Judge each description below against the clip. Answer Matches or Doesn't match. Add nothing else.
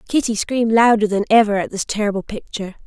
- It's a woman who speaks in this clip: Matches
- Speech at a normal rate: Matches